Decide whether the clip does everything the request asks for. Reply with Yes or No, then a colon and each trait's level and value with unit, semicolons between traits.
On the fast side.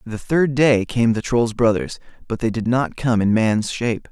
Yes: fast, 220 wpm